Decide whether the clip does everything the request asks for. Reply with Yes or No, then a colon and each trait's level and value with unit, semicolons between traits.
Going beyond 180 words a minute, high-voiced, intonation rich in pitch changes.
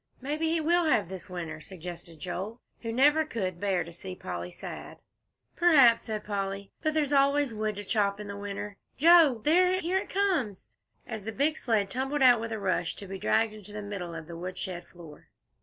Yes: average, 200 wpm; high, 210 Hz; wide, 7.2 semitones